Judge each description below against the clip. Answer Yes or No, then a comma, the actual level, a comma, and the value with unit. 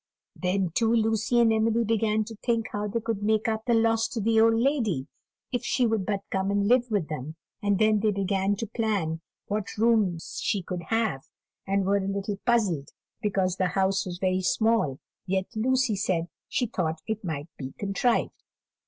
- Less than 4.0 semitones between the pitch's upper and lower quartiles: Yes, average, 3.0 semitones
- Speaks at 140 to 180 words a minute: No, average, 190 wpm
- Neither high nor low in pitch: No, high, 205 Hz